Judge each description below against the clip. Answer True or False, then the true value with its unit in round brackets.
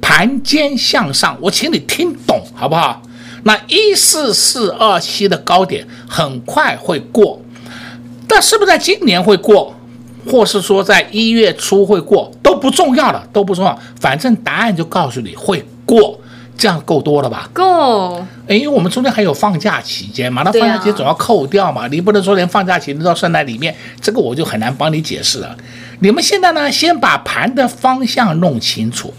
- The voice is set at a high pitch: True (200 Hz)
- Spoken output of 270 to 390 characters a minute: True (275 characters per minute)